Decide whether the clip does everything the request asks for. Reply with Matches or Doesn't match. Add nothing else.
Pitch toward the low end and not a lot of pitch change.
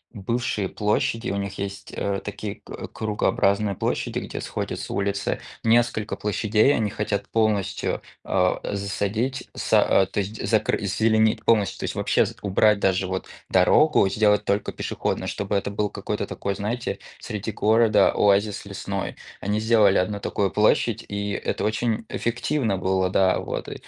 Matches